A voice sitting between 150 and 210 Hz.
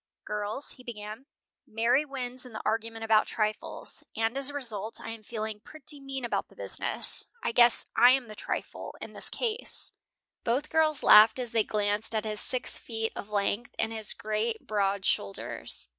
No: high, 225 Hz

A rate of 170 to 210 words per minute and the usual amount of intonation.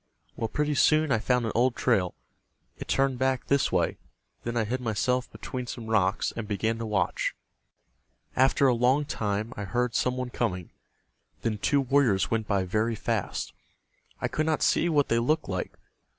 Yes: average, 180 wpm; average, 3.6 semitones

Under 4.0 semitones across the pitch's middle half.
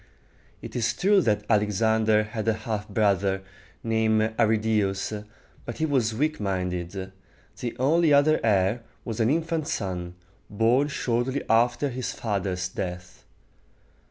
Yes: average, 3.5 semitones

